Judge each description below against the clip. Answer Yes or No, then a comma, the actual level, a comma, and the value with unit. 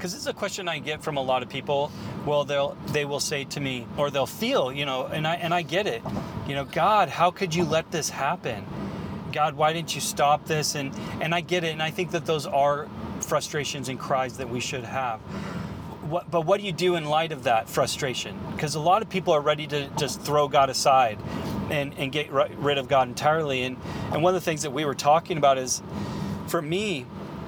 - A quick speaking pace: Yes, fast, 235 wpm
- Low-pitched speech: No, medium, 150 Hz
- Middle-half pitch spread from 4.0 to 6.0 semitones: No, average, 3.5 semitones